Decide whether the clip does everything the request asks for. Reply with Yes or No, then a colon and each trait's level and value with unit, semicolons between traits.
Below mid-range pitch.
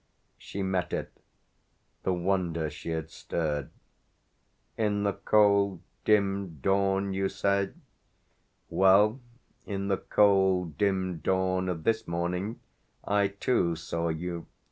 Yes: very low, 95 Hz